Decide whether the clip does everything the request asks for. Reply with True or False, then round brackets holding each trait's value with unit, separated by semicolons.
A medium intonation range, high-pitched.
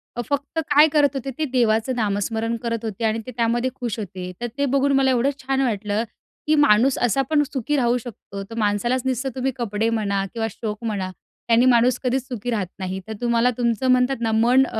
True (3.1 semitones; 235 Hz)